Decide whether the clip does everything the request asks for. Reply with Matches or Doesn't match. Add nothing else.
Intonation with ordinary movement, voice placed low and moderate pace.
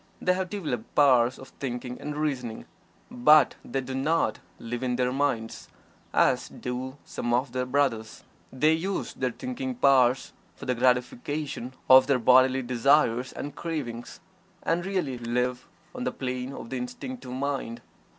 Matches